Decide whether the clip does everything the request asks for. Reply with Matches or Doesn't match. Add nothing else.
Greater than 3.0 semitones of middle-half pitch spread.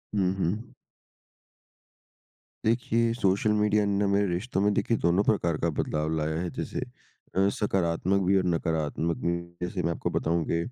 Matches